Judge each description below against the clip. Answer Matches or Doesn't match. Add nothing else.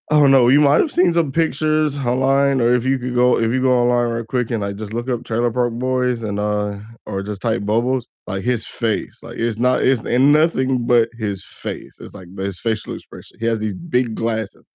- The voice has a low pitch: Matches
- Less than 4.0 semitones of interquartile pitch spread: Matches